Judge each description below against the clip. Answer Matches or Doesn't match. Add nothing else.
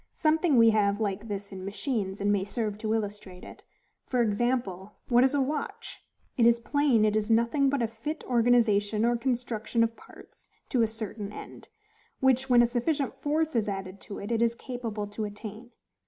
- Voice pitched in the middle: Doesn't match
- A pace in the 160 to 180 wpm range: Doesn't match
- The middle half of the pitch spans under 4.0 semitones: Matches